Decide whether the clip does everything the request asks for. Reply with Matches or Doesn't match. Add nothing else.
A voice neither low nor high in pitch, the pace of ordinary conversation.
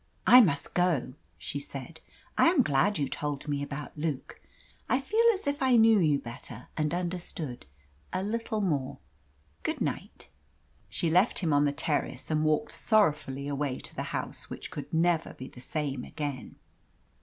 Matches